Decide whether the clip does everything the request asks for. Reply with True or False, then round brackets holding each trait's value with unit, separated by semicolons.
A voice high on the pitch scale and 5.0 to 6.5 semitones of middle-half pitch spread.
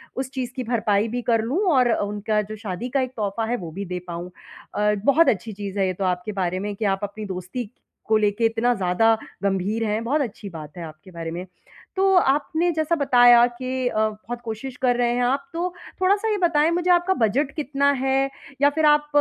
True (230 Hz; 5.3 semitones)